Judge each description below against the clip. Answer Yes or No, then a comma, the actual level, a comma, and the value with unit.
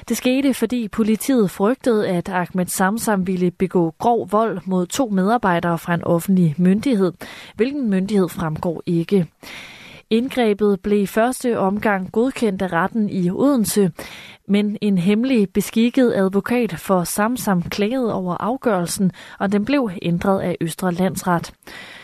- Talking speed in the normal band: No, slow, 135 wpm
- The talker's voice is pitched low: No, high, 200 Hz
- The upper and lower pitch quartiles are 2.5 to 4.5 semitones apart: Yes, average, 3.8 semitones